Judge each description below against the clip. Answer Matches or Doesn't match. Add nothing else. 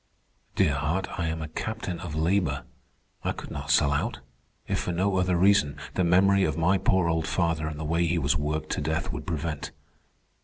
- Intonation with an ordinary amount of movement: Matches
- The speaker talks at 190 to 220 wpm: Matches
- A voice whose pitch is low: Matches